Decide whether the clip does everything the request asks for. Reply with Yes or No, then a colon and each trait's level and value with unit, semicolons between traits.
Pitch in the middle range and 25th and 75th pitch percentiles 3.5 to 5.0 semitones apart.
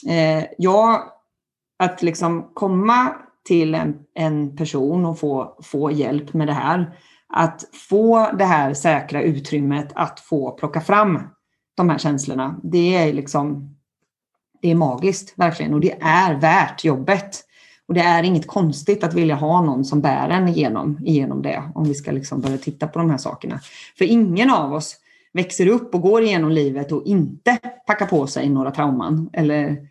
Yes: medium, 160 Hz; average, 3.8 semitones